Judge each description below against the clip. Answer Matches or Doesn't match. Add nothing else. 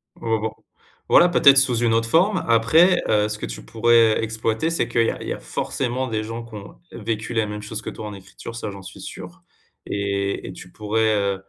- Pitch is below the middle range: Matches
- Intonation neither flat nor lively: Doesn't match